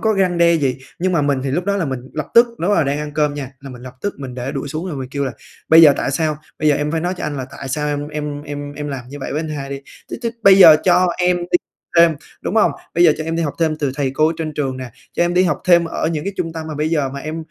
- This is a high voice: No, medium, 150 Hz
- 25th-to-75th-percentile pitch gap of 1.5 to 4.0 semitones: Yes, average, 3.3 semitones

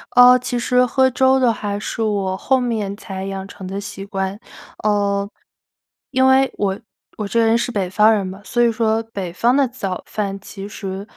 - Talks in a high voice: Yes, high, 210 Hz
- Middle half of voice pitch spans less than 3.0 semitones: No, average, 3.7 semitones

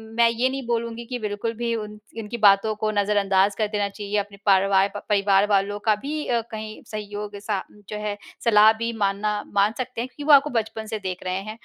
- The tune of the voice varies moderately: No, narrow, 2.3 semitones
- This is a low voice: No, high, 210 Hz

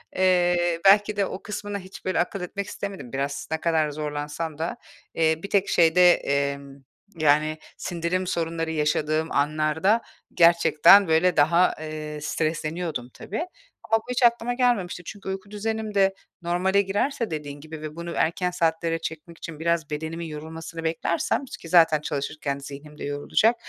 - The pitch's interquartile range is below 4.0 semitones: Yes, average, 3.5 semitones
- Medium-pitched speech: Yes, medium, 165 Hz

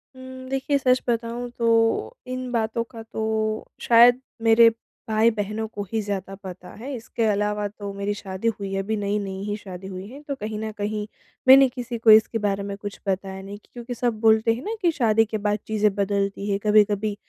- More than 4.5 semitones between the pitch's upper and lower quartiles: No, narrow, 2.4 semitones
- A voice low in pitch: No, high, 215 Hz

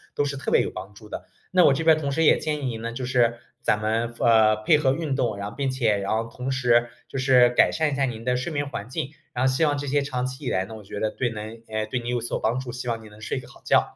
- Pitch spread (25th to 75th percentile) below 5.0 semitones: Yes, average, 3.3 semitones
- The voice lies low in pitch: Yes, low, 125 Hz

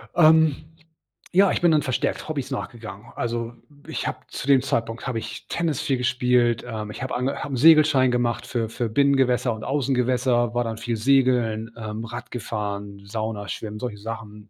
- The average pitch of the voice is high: No, low, 120 Hz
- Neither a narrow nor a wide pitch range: Yes, average, 3.1 semitones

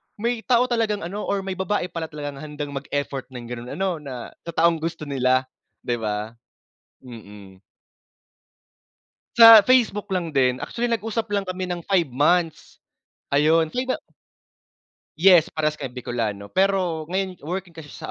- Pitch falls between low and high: Yes, medium, 165 Hz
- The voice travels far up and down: Yes, wide, 6.2 semitones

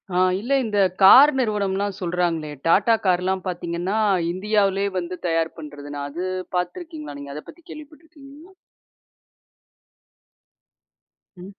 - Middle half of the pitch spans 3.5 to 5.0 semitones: Yes, average, 4.7 semitones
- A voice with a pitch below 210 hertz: Yes, high, 190 Hz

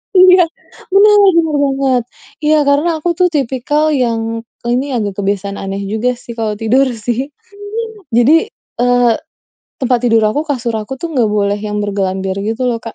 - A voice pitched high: Yes, high, 245 Hz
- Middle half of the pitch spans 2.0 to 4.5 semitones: No, average, 4.9 semitones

